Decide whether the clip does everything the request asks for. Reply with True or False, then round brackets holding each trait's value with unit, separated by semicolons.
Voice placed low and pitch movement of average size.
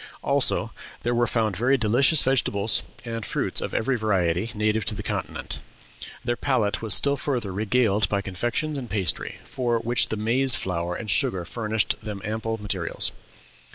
True (110 Hz; 3.0 semitones)